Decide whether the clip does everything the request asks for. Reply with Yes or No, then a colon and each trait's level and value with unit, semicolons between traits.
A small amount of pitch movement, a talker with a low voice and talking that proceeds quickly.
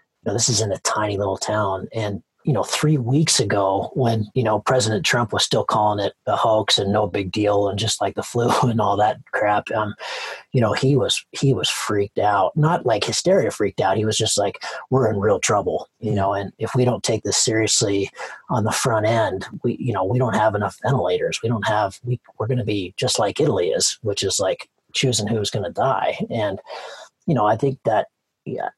No: average, 3.7 semitones; low, 110 Hz; fast, 225 wpm